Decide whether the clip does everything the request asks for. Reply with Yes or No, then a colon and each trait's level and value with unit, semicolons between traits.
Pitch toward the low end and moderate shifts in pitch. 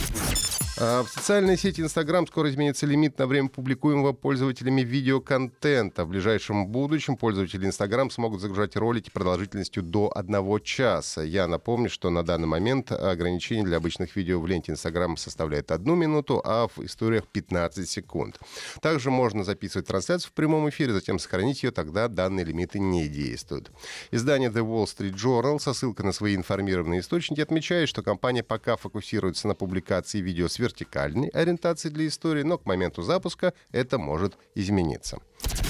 No: low, 110 Hz; wide, 7.0 semitones